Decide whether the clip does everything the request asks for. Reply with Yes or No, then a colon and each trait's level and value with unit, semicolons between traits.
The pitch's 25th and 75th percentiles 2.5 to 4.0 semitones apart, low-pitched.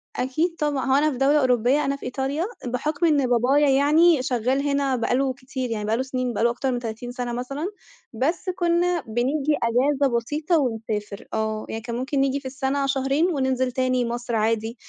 No: average, 2.9 semitones; very high, 260 Hz